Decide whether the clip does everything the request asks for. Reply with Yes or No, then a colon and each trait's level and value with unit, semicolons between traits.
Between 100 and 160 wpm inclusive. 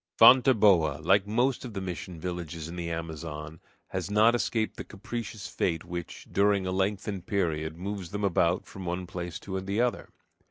No: average, 170 wpm